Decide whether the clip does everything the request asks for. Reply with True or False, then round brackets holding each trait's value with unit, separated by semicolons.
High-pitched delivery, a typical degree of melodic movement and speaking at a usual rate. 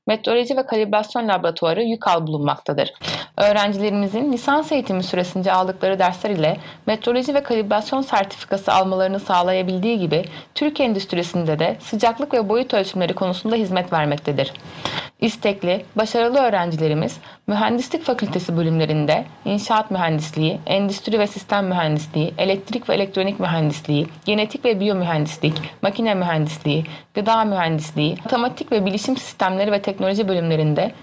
True (195 Hz; 4.8 semitones; 115 wpm)